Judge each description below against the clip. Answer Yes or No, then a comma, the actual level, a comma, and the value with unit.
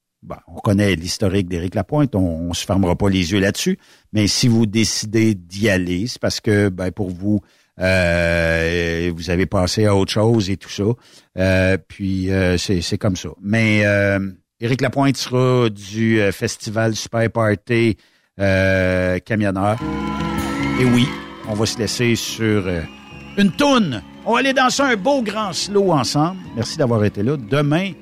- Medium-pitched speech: No, low, 105 Hz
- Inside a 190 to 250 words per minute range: No, average, 165 wpm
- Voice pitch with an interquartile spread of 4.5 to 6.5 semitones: No, average, 4.1 semitones